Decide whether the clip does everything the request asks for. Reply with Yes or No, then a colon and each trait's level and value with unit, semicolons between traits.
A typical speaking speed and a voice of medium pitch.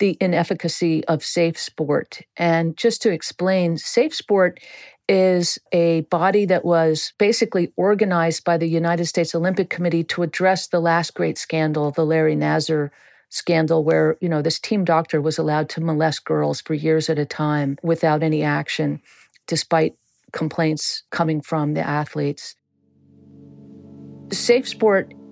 Yes: average, 145 wpm; medium, 165 Hz